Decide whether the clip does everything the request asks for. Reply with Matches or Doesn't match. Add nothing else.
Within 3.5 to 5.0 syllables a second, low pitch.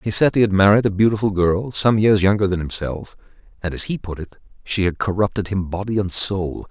Doesn't match